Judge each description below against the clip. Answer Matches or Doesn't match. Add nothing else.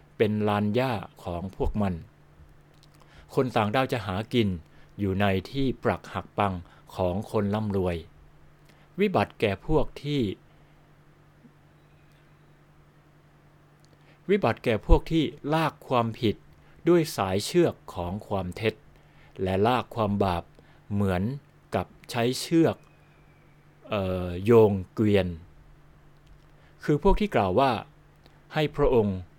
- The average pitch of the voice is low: Matches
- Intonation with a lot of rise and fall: Matches